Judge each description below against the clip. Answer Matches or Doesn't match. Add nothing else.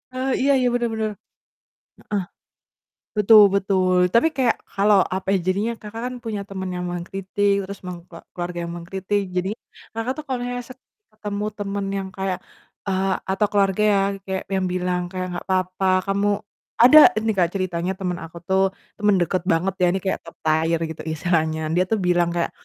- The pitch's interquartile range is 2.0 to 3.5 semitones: Matches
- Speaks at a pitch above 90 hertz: Matches